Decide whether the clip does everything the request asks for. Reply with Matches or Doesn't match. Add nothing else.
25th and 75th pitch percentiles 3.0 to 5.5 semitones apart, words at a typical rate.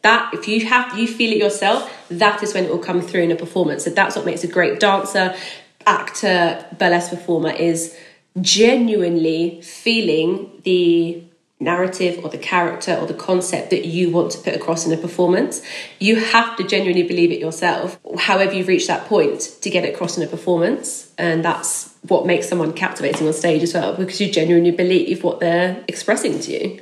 Doesn't match